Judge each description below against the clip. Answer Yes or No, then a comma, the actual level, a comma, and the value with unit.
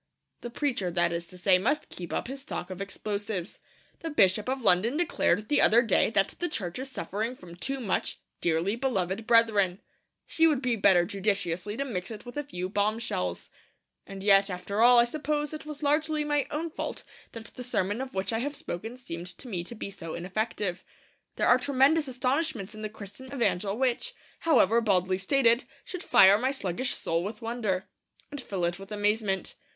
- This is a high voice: Yes, high, 220 Hz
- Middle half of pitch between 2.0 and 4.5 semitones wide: No, wide, 5.6 semitones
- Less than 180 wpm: No, average, 190 wpm